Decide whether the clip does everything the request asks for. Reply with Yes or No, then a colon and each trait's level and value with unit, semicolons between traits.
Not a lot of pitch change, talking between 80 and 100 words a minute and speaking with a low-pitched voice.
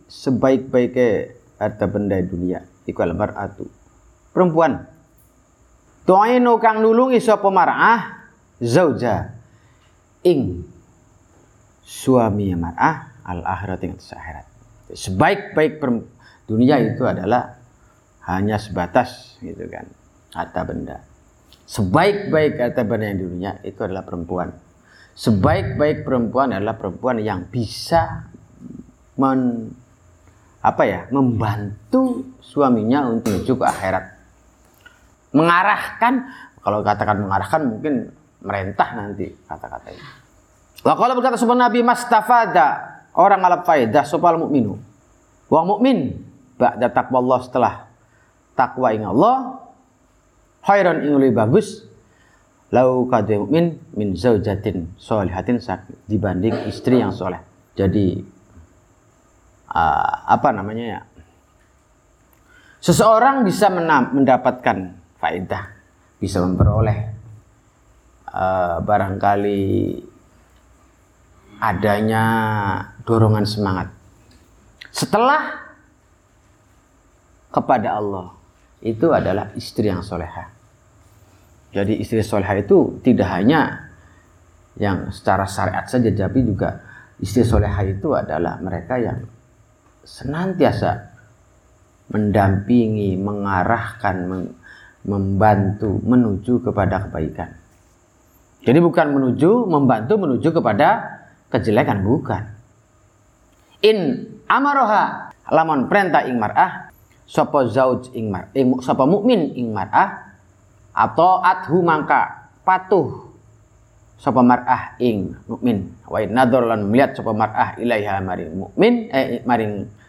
No: average, 5.3 semitones; average, 90 wpm; low, 110 Hz